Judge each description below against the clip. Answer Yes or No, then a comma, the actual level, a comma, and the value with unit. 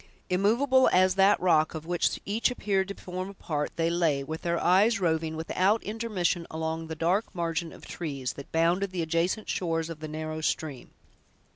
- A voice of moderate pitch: Yes, medium, 170 Hz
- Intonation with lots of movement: No, average, 3.2 semitones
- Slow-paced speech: No, average, 180 wpm